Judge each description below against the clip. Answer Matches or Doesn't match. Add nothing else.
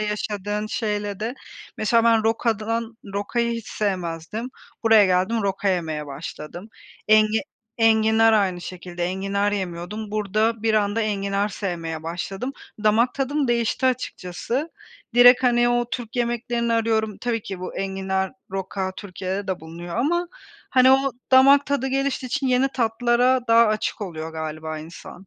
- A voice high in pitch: Matches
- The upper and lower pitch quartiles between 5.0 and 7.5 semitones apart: Doesn't match